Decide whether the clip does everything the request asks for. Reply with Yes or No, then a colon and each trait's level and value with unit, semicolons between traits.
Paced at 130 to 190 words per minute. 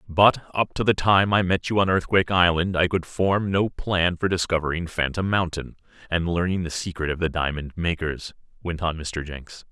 No: average, 200 wpm